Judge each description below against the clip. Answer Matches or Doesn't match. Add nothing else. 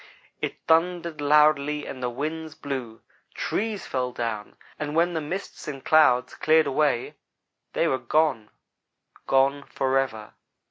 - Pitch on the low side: Doesn't match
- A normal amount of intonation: Matches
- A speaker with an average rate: Doesn't match